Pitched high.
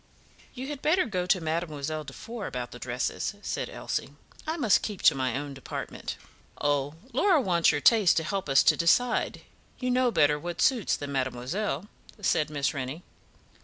No: medium, 165 Hz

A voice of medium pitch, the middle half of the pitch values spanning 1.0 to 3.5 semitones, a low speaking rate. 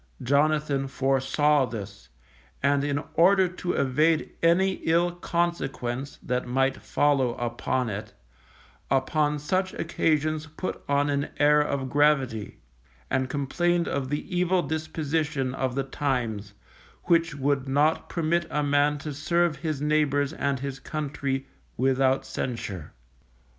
Yes: medium, 145 Hz; average, 2.9 semitones; slow, 125 wpm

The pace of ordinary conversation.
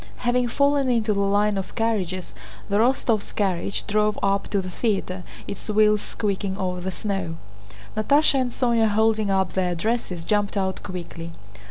Yes: average, 160 wpm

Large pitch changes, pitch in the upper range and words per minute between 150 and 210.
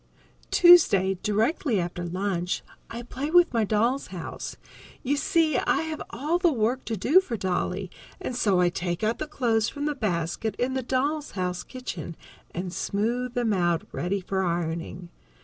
Yes: wide, 6.6 semitones; high, 220 Hz; average, 170 wpm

